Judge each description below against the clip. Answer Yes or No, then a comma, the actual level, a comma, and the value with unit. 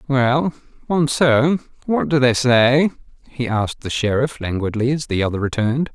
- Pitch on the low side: Yes, low, 130 Hz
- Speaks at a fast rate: No, average, 150 wpm